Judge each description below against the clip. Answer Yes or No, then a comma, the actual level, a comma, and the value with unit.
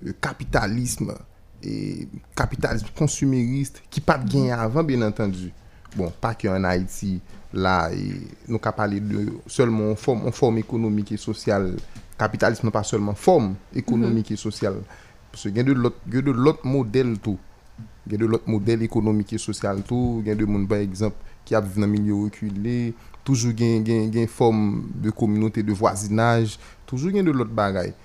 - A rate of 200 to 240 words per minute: No, average, 150 wpm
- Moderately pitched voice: No, low, 110 Hz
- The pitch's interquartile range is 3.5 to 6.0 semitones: No, narrow, 2.5 semitones